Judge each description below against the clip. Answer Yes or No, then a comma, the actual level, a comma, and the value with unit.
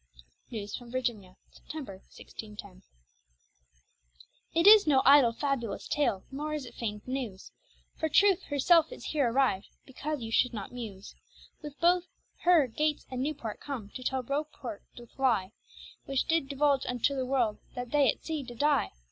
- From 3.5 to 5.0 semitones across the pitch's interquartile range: Yes, average, 4.5 semitones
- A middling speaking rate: Yes, average, 160 wpm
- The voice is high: Yes, very high, 265 Hz